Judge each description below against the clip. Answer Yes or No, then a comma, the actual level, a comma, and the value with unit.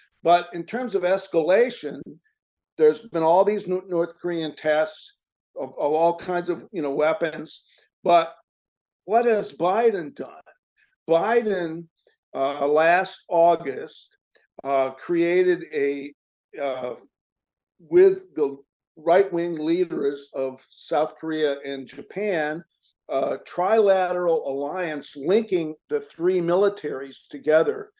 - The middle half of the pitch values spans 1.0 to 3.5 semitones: No, average, 4.0 semitones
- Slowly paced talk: Yes, slow, 110 wpm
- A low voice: No, medium, 170 Hz